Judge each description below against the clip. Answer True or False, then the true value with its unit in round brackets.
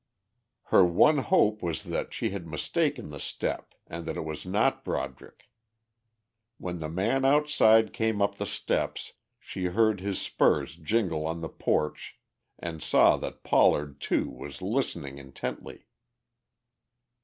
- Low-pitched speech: True (90 Hz)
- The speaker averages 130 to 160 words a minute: True (140 wpm)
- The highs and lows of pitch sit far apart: True (6.0 semitones)